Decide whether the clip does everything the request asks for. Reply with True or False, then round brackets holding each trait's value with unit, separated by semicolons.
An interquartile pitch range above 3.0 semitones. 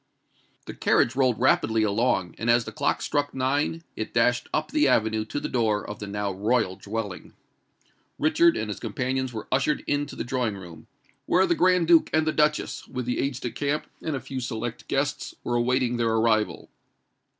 True (4.6 semitones)